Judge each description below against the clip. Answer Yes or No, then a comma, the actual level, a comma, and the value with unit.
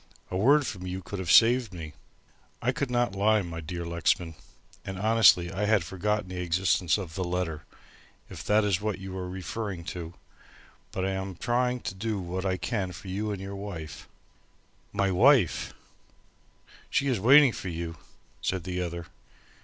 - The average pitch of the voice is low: Yes, very low, 95 Hz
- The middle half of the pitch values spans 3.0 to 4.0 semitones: Yes, average, 3.3 semitones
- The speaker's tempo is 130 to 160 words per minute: No, average, 175 wpm